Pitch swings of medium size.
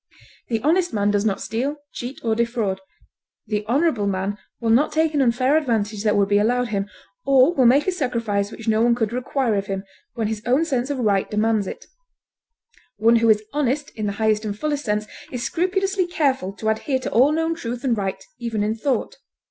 Yes: average, 4.6 semitones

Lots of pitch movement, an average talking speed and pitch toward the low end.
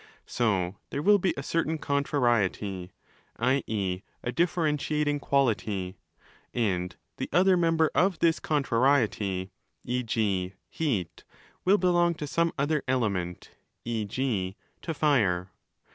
No: wide, 8.0 semitones; slow, 110 wpm; low, 125 Hz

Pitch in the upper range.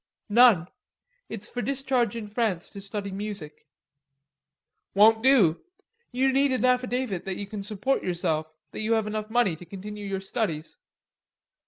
Yes: high, 210 Hz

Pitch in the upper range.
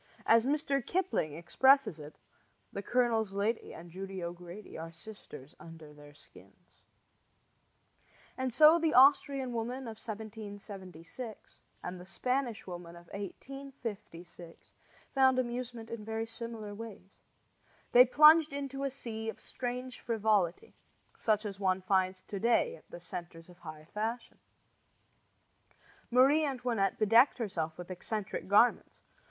Yes: high, 220 Hz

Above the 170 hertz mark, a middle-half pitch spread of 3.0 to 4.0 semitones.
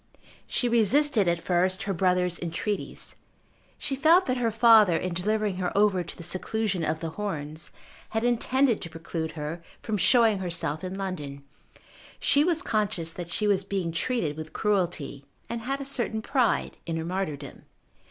No: high, 190 Hz; average, 5.1 semitones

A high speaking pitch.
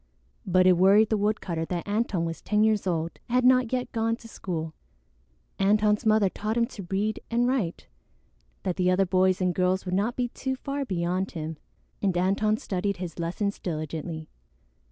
Yes: high, 195 Hz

